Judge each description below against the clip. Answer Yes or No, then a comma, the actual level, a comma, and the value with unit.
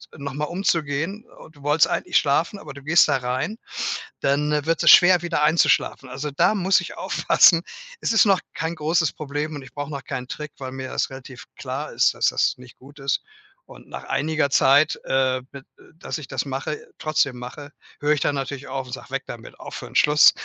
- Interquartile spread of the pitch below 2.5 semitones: No, average, 2.9 semitones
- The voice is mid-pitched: Yes, medium, 145 Hz